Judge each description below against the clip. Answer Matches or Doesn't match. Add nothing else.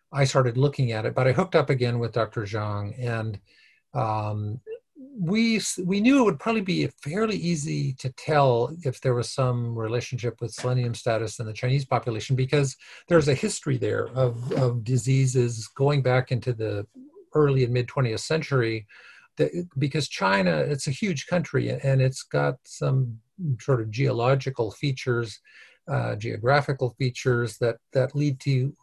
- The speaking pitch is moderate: Doesn't match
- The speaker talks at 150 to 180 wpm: Matches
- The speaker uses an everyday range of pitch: Matches